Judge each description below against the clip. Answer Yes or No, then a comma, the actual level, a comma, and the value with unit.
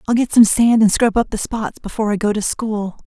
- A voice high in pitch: Yes, high, 215 Hz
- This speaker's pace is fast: Yes, fast, 275 wpm